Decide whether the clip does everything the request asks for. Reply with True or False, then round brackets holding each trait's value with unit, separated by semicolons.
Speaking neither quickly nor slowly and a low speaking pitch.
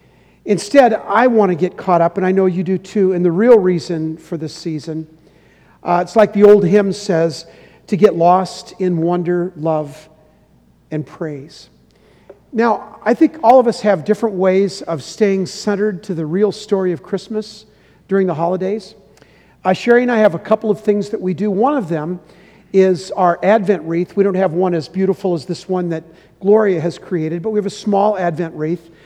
False (195 wpm; 185 Hz)